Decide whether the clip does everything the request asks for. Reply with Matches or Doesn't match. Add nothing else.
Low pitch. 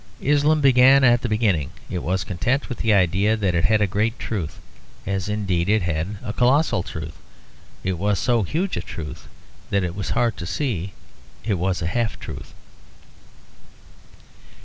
Matches